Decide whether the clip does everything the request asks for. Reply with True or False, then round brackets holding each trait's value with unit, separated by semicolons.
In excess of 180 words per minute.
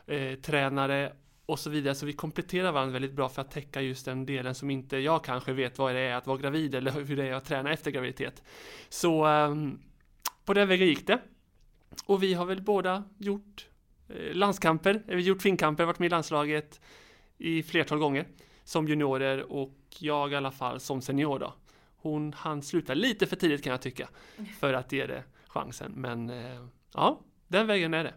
True (195 wpm)